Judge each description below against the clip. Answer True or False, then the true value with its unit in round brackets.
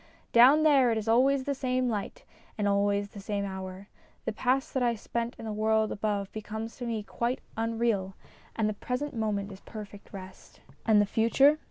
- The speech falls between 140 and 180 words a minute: False (190 wpm)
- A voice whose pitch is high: True (220 Hz)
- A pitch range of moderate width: True (3.3 semitones)